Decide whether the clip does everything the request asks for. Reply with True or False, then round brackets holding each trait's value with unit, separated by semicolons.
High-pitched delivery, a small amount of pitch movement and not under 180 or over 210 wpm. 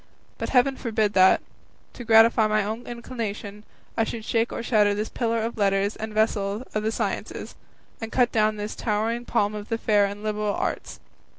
True (215 Hz; 1.7 semitones; 185 wpm)